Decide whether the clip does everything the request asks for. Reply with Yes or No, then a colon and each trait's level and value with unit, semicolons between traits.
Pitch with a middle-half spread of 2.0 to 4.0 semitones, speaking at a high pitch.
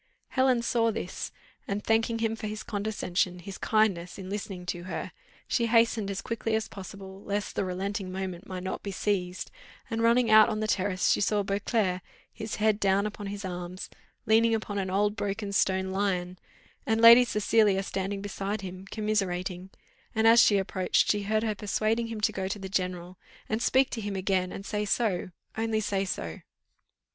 Yes: narrow, 2.6 semitones; high, 205 Hz